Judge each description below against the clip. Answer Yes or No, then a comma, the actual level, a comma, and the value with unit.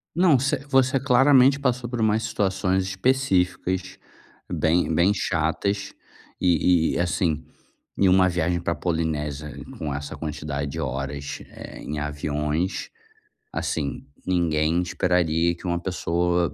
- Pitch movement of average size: Yes, average, 4.1 semitones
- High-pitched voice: No, very low, 90 Hz